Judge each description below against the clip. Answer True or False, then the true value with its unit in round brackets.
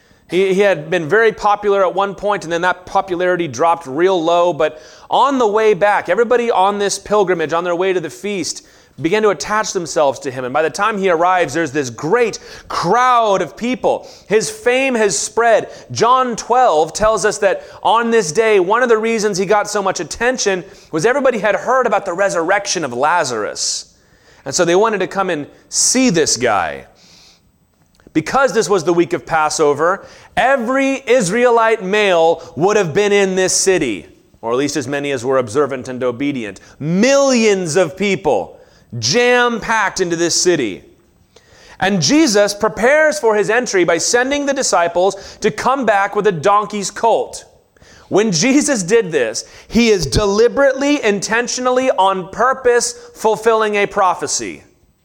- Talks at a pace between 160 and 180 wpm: True (165 wpm)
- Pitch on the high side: True (205 Hz)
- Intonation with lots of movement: False (4.8 semitones)